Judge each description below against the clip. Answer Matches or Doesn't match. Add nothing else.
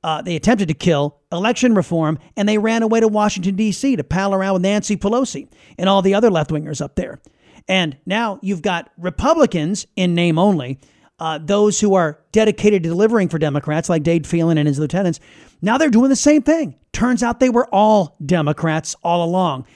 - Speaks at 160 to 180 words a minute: Doesn't match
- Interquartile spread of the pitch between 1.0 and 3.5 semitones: Doesn't match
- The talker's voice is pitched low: Doesn't match